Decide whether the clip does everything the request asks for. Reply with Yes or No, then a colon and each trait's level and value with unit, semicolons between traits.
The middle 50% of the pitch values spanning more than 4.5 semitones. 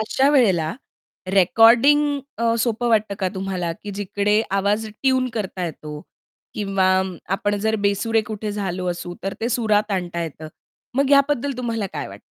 No: average, 3.5 semitones